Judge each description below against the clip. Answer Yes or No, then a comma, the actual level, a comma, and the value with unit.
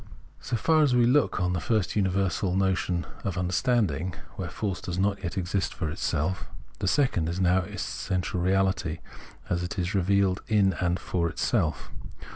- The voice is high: No, very low, 95 Hz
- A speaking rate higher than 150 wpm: Yes, average, 180 wpm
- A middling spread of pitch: No, narrow, 2.1 semitones